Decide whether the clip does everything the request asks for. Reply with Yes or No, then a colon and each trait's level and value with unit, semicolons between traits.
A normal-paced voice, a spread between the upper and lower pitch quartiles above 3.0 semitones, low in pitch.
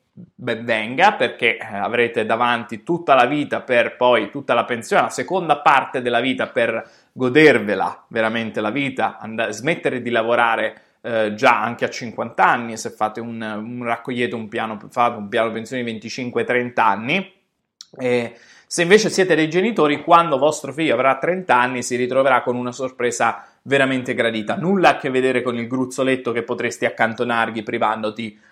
No: average, 160 wpm; average, 2.7 semitones; low, 120 Hz